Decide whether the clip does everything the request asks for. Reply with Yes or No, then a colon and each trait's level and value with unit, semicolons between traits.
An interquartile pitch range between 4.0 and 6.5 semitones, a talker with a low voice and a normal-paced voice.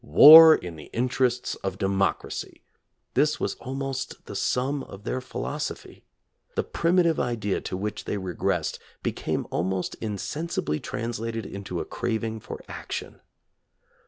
No: wide, 5.4 semitones; low, 115 Hz; slow, 130 wpm